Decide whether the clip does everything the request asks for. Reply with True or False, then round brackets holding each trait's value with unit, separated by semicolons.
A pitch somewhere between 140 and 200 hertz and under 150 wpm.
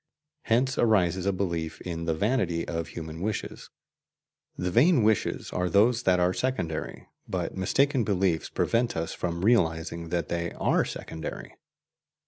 False (90 Hz; 140 wpm)